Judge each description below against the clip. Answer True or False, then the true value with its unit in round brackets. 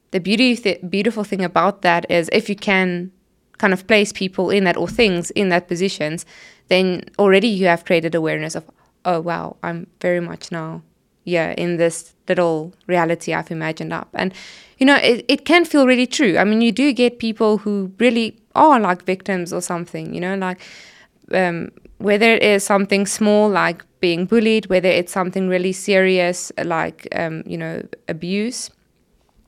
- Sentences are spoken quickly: False (175 wpm)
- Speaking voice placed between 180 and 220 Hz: True (190 Hz)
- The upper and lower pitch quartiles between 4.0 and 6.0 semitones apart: False (3.5 semitones)